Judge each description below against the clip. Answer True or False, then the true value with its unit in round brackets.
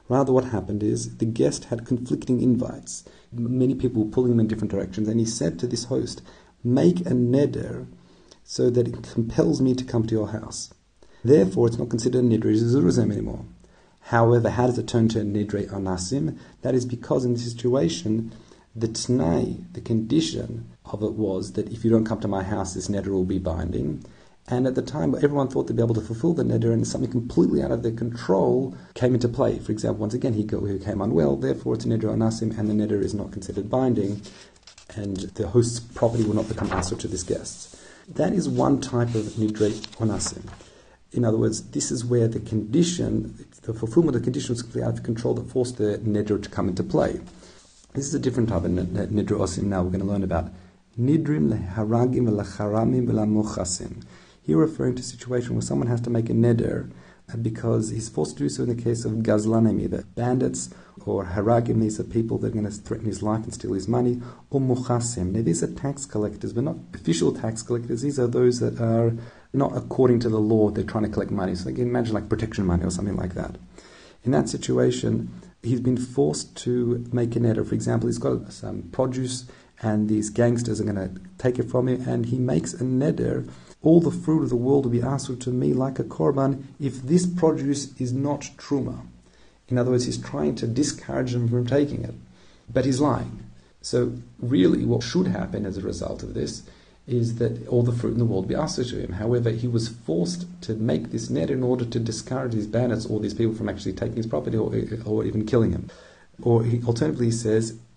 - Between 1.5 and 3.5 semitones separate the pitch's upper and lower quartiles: True (3.2 semitones)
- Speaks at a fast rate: True (210 wpm)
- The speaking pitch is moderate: False (115 Hz)